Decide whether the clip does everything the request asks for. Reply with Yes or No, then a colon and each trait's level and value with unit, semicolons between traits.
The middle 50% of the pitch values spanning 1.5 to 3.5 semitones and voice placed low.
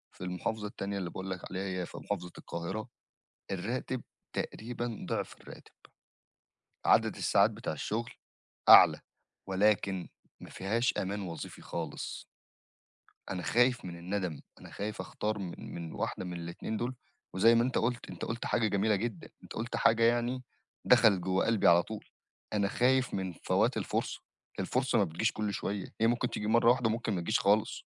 No: average, 3.9 semitones; low, 105 Hz